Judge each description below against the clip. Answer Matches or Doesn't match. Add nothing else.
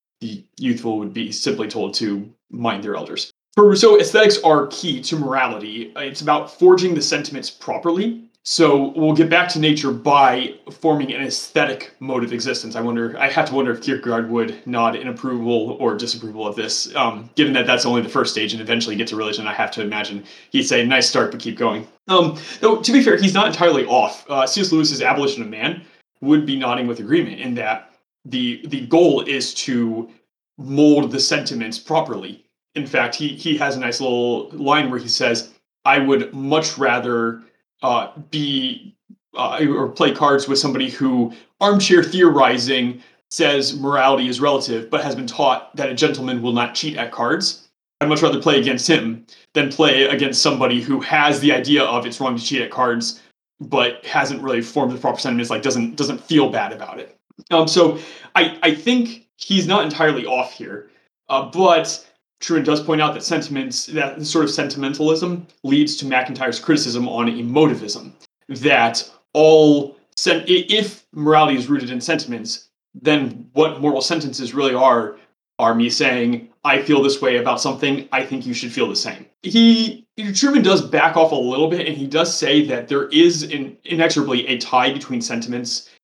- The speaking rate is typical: Matches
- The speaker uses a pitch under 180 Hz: Matches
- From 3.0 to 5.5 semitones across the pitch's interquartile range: Matches